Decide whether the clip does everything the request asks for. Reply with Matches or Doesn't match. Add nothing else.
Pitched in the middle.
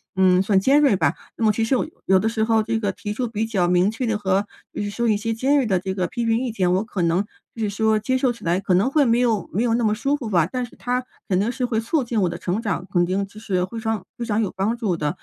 Doesn't match